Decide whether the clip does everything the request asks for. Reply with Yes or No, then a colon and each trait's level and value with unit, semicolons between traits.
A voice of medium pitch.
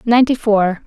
No: high, 220 Hz